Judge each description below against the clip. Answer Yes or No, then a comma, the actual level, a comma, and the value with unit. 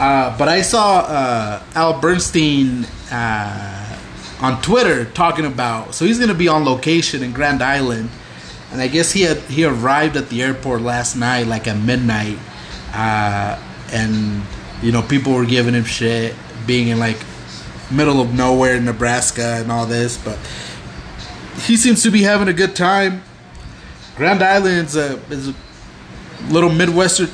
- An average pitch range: No, wide, 5.7 semitones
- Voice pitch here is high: No, low, 125 Hz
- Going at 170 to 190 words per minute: No, average, 160 wpm